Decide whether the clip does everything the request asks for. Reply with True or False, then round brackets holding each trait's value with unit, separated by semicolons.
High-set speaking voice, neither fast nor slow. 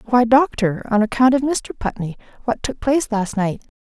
True (235 Hz; 175 wpm)